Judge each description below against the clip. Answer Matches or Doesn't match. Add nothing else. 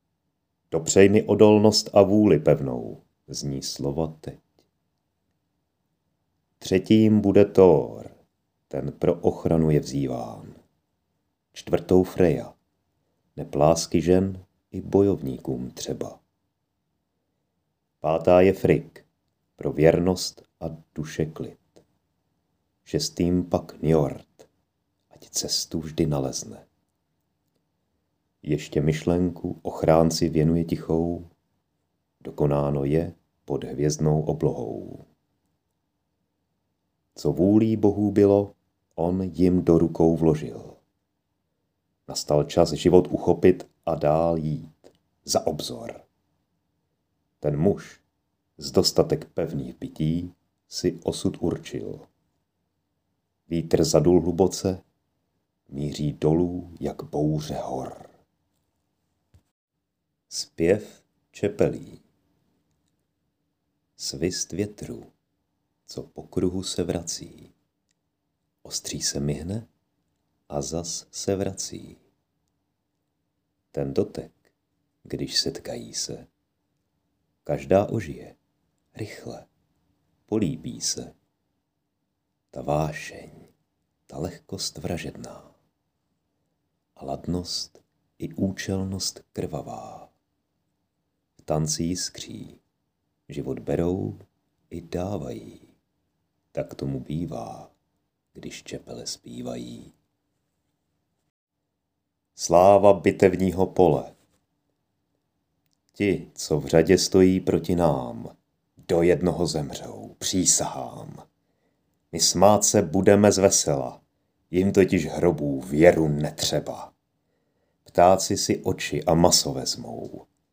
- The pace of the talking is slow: Matches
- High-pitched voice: Doesn't match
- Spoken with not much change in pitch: Doesn't match